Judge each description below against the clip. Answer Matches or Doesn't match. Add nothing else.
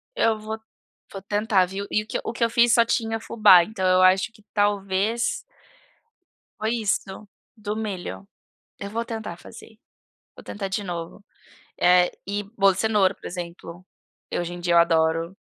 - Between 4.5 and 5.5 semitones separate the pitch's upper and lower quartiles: Doesn't match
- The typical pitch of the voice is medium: Doesn't match